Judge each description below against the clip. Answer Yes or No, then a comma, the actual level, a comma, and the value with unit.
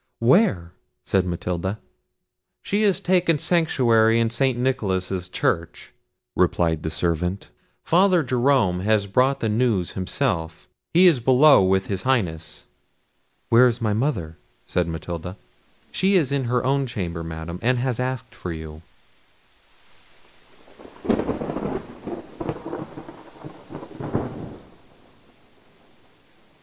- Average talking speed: No, slow, 100 wpm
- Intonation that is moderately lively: No, wide, 6.9 semitones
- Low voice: Yes, low, 110 Hz